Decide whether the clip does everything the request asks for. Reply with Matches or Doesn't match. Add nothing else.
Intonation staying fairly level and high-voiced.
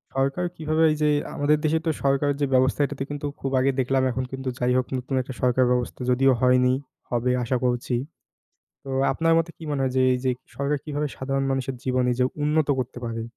Doesn't match